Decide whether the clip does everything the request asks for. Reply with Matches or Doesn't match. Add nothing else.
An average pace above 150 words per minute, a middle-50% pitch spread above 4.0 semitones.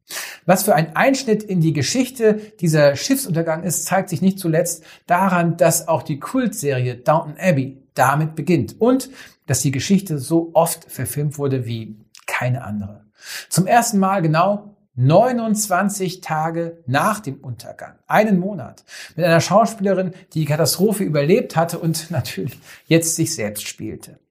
Doesn't match